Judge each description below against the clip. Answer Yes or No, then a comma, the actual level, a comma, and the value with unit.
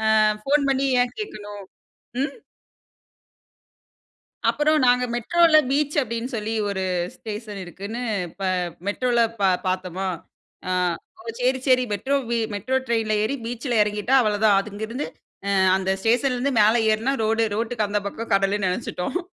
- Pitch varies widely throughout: No, average, 3.9 semitones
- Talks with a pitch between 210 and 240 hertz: Yes, high, 225 Hz